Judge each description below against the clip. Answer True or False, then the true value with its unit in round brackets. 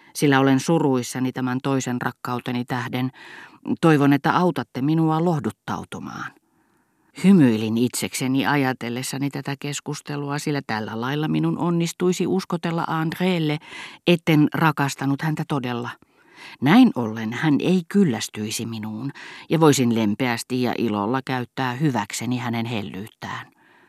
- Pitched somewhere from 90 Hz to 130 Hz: False (140 Hz)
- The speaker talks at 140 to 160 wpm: False (110 wpm)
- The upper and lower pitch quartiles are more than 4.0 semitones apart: True (4.5 semitones)